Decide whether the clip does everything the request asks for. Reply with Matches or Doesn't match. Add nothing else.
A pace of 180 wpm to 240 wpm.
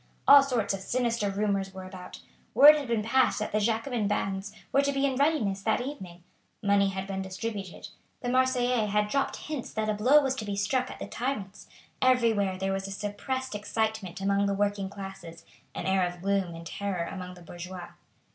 Matches